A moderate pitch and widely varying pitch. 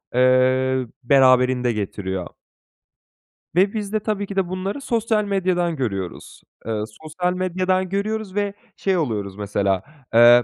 Yes: medium, 160 Hz; wide, 8.3 semitones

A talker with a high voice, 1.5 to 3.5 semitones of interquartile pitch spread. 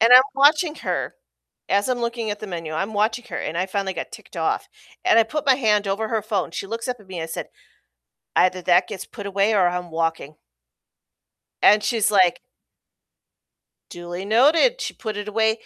No: high, 210 Hz; average, 3.9 semitones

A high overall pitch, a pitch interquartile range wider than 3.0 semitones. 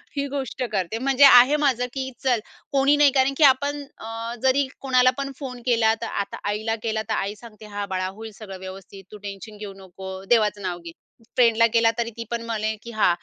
Yes: high, 230 Hz; average, 4.0 semitones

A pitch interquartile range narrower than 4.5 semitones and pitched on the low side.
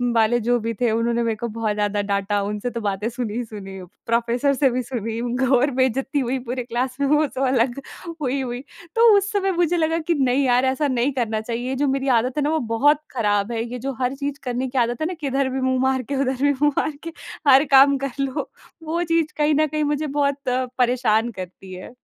No: average, 3.3 semitones; very high, 255 Hz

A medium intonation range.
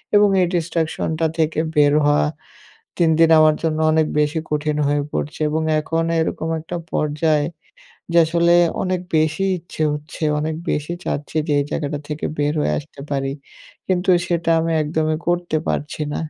No: narrow, 1.9 semitones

